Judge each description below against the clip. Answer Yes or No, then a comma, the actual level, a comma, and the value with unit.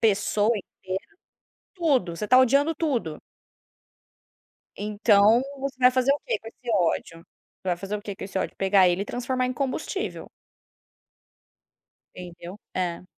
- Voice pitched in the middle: No, high, 210 Hz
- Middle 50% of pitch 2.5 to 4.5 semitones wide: No, average, 5.3 semitones